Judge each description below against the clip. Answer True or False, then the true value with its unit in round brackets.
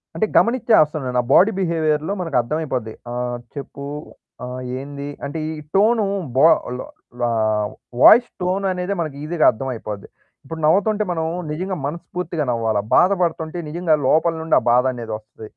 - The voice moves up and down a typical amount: False (5.9 semitones)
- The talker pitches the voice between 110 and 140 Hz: False (155 Hz)